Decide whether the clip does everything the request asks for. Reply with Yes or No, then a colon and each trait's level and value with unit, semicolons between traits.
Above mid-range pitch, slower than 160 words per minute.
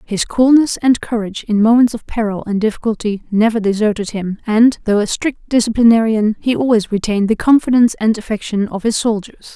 No: high, 220 Hz; average, 175 wpm